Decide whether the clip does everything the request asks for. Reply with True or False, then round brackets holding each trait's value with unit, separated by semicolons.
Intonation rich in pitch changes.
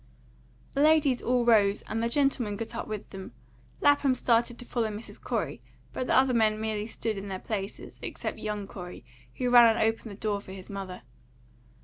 False (3.2 semitones)